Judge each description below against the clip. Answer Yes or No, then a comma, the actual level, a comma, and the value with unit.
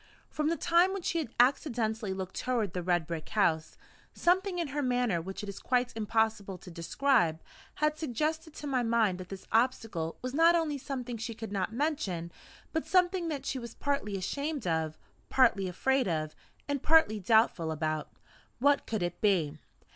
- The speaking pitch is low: No, high, 230 Hz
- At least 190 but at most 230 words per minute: No, average, 175 wpm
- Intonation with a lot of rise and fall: Yes, wide, 7.5 semitones